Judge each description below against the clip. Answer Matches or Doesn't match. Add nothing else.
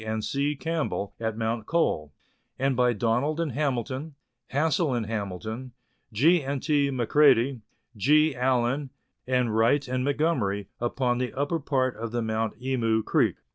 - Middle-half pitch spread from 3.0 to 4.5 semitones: Matches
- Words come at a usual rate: Matches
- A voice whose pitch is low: Matches